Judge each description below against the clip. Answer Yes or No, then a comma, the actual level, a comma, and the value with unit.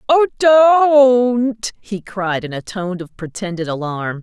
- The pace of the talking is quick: No, average, 140 wpm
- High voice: Yes, high, 210 Hz